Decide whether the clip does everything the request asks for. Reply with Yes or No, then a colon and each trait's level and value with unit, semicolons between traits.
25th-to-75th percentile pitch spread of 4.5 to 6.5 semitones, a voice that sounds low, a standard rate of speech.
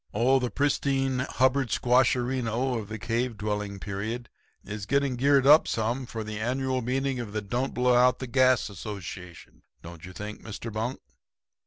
No: average, 3.5 semitones; low, 120 Hz; average, 165 wpm